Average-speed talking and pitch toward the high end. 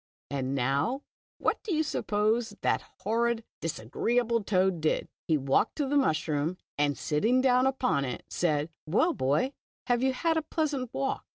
Yes: average, 165 wpm; high, 220 Hz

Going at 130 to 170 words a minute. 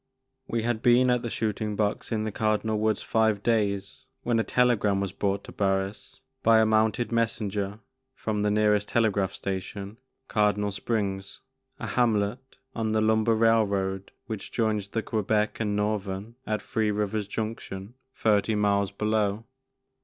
Yes: average, 155 wpm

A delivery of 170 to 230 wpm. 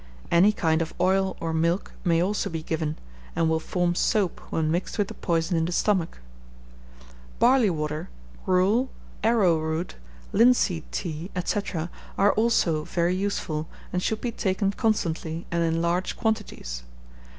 No: average, 145 wpm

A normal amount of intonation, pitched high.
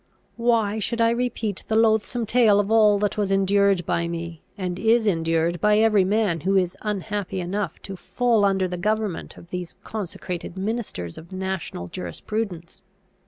Yes: average, 3.6 semitones; high, 200 Hz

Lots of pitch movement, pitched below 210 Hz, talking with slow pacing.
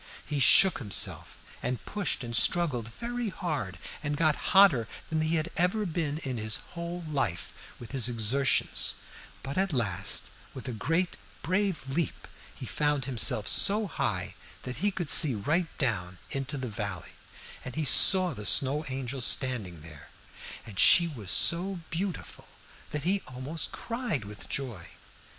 No: wide, 6.6 semitones; medium, 140 Hz; average, 155 wpm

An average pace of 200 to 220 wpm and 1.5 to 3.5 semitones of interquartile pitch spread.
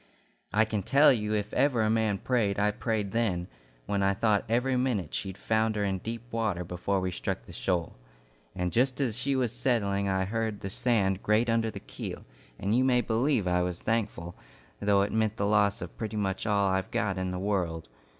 Yes: fast, 205 wpm; average, 3.0 semitones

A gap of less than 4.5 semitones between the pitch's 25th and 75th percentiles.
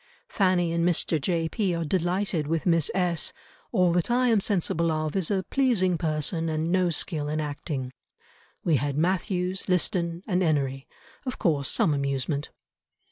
Yes: average, 3.2 semitones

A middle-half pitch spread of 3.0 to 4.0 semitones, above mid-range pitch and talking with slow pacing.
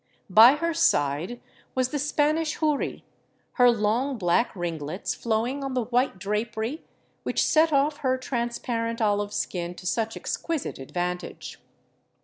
No: average, 5.3 semitones; high, 235 Hz; slow, 130 wpm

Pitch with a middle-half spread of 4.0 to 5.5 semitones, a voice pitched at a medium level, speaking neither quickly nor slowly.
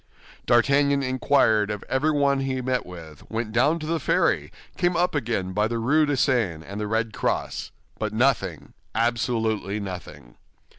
No: average, 4.7 semitones; low, 120 Hz; average, 155 wpm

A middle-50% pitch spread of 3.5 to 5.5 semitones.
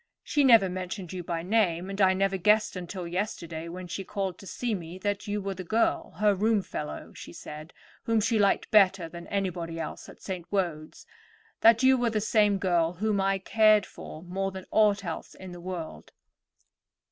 No: average, 3.0 semitones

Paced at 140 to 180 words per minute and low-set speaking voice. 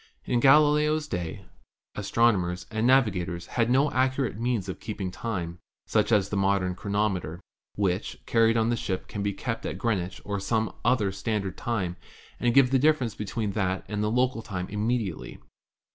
Yes: average, 175 wpm; low, 105 Hz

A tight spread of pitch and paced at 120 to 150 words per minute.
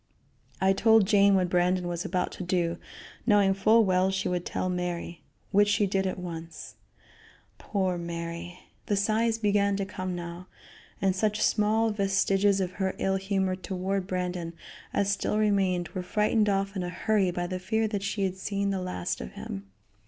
No: narrow, 2.0 semitones; average, 175 wpm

